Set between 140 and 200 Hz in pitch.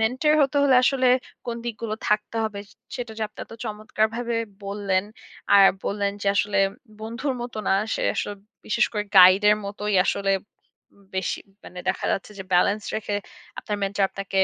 No: high, 210 Hz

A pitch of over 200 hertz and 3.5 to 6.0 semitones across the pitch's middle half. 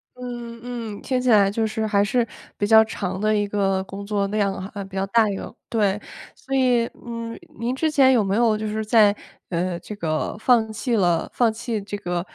No: high, 215 Hz; average, 2.8 semitones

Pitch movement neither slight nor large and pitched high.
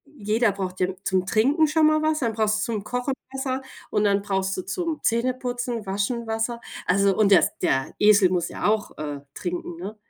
Yes: average, 4.3 semitones; high, 215 Hz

